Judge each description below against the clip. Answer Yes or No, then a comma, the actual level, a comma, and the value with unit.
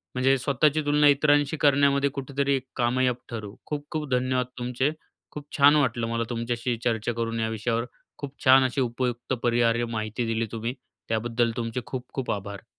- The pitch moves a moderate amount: Yes, average, 3.2 semitones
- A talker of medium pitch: No, low, 125 Hz